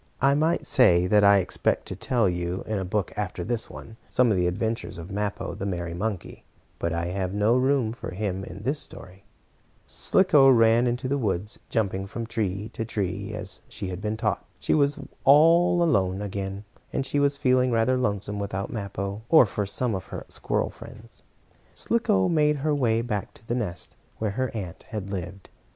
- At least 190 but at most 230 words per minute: Yes, average, 195 wpm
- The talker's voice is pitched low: Yes, low, 105 Hz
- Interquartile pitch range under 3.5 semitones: No, average, 4.7 semitones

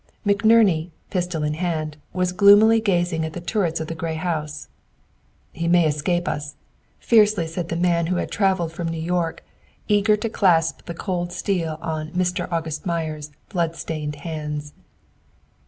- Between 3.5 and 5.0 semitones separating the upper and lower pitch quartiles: No, narrow, 2.4 semitones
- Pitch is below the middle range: No, medium, 170 Hz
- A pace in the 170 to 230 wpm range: No, average, 155 wpm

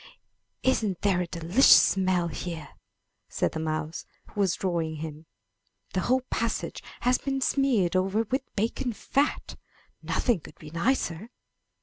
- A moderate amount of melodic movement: No, wide, 6.4 semitones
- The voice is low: No, high, 190 Hz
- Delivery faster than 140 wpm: No, slow, 135 wpm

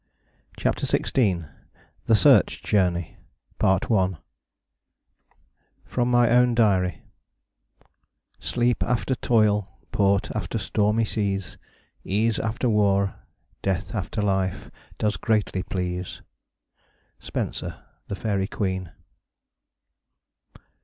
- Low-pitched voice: Yes, low, 100 Hz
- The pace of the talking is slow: Yes, slow, 85 wpm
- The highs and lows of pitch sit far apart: No, average, 3.1 semitones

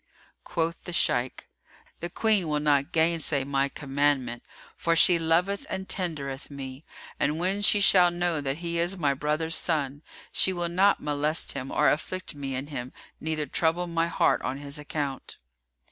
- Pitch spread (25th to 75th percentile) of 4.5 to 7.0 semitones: No, average, 3.5 semitones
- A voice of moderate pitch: Yes, medium, 155 Hz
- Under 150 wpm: No, average, 165 wpm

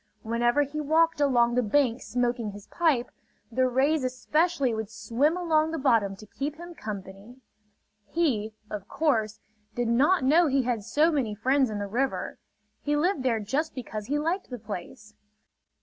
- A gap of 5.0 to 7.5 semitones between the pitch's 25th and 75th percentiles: Yes, average, 5.3 semitones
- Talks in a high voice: Yes, very high, 255 Hz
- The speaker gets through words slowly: No, average, 165 wpm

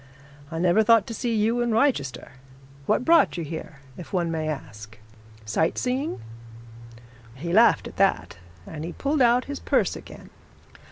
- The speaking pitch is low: No, medium, 185 Hz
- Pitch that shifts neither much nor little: No, wide, 7.3 semitones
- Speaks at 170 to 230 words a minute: No, average, 160 wpm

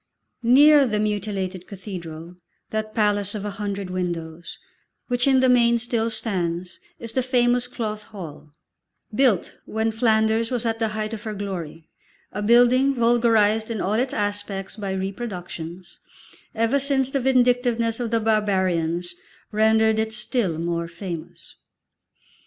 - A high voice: Yes, high, 215 Hz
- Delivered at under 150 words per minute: Yes, average, 140 wpm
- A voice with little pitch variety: No, average, 3.7 semitones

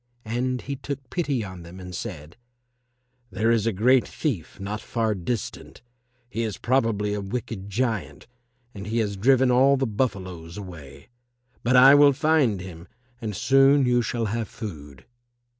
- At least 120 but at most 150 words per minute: No, average, 160 wpm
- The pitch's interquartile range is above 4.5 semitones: Yes, average, 5.0 semitones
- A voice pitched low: Yes, low, 110 Hz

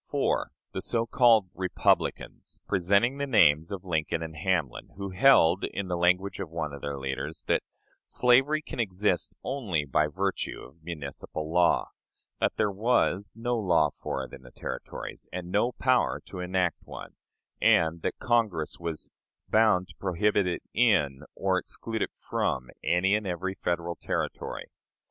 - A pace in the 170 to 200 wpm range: No, average, 160 wpm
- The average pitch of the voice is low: Yes, very low, 90 Hz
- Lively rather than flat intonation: No, average, 4.5 semitones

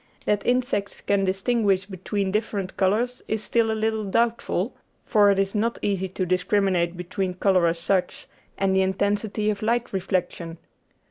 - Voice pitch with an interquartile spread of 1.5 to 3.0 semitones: Yes, narrow, 2.5 semitones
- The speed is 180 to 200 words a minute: No, average, 155 wpm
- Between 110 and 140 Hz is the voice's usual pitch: No, high, 200 Hz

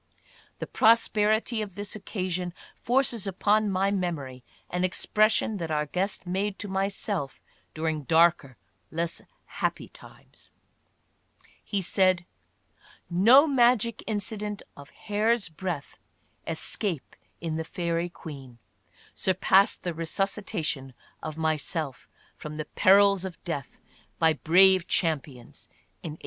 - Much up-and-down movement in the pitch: No, average, 4.2 semitones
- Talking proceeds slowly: Yes, slow, 125 wpm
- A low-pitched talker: No, medium, 185 Hz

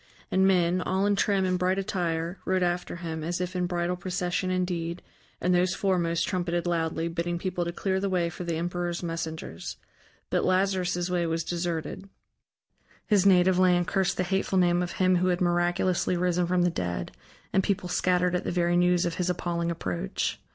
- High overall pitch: No, medium, 175 Hz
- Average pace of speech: Yes, average, 185 wpm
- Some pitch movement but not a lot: No, narrow, 1.2 semitones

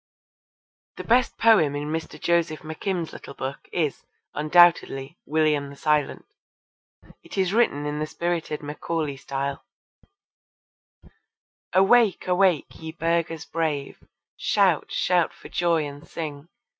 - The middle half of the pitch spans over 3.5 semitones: No, average, 2.9 semitones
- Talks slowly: Yes, slow, 120 wpm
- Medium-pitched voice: Yes, medium, 160 Hz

